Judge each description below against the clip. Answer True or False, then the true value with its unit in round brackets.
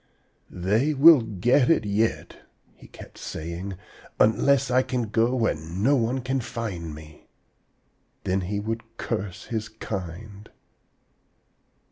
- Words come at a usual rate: False (120 wpm)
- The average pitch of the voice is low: True (110 Hz)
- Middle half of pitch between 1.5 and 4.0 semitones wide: False (4.6 semitones)